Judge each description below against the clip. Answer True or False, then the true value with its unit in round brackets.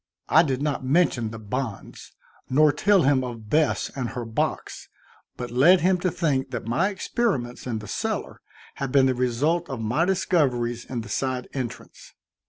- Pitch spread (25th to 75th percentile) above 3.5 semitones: True (4.9 semitones)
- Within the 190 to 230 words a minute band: False (175 wpm)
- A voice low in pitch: True (130 Hz)